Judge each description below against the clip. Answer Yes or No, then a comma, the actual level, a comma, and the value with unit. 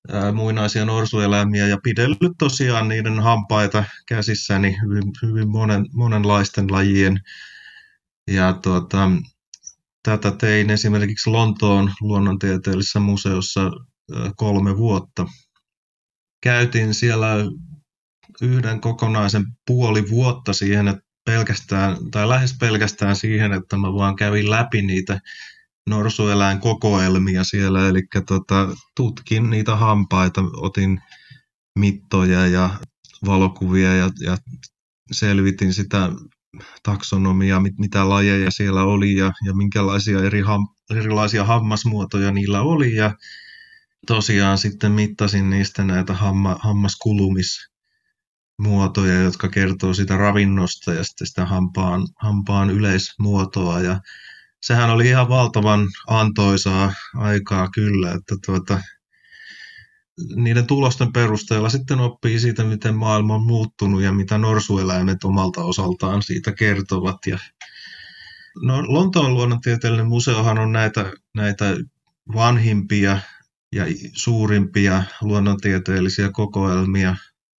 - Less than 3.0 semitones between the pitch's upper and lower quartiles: Yes, narrow, 2.6 semitones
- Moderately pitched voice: No, low, 105 Hz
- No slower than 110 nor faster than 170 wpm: No, average, 100 wpm